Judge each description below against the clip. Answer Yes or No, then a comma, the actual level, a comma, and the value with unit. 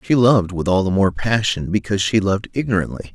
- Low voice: Yes, low, 100 Hz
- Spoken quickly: Yes, fast, 210 wpm